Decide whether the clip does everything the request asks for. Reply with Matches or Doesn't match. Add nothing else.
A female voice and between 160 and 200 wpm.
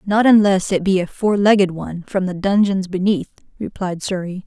Matches